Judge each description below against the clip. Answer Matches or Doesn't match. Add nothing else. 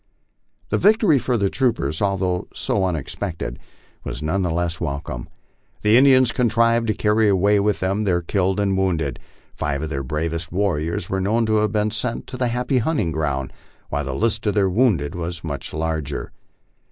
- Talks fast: Doesn't match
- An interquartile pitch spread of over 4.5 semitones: Matches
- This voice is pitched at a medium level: Doesn't match